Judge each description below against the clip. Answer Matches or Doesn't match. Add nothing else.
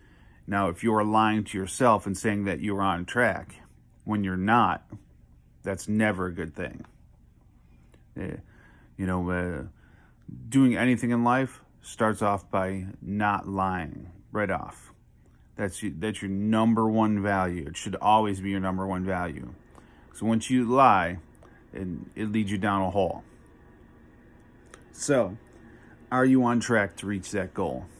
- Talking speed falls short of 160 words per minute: Matches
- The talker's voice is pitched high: Doesn't match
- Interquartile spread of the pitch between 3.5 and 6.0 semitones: Doesn't match